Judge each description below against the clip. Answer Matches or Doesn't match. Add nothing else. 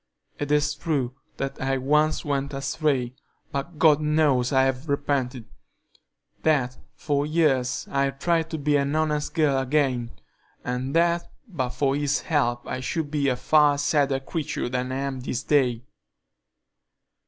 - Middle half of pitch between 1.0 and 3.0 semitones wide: Matches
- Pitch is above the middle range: Doesn't match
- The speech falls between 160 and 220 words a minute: Doesn't match